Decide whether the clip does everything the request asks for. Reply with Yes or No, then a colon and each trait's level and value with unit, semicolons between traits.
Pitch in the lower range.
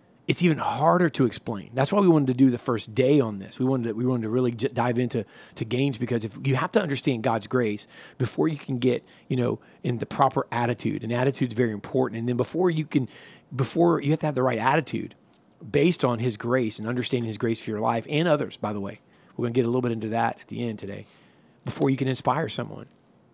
Yes: low, 125 Hz